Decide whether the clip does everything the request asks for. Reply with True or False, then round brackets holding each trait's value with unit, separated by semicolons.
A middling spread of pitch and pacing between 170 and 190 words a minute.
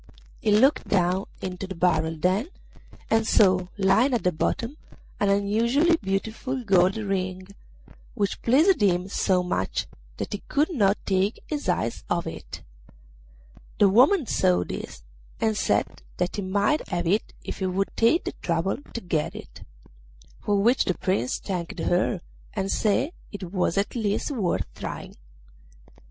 False (3.7 semitones; 150 wpm)